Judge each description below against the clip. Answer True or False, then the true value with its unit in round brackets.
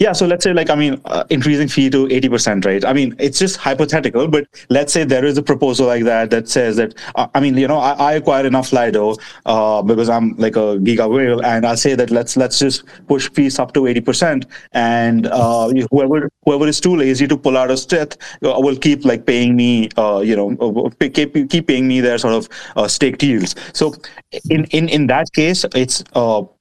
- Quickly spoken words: True (220 wpm)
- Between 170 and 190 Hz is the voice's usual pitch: False (135 Hz)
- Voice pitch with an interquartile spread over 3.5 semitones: True (4.0 semitones)